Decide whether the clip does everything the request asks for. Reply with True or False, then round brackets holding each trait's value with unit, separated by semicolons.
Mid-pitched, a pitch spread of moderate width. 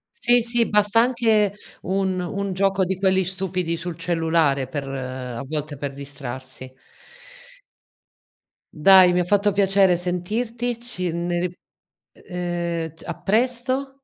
True (180 Hz; 4.0 semitones)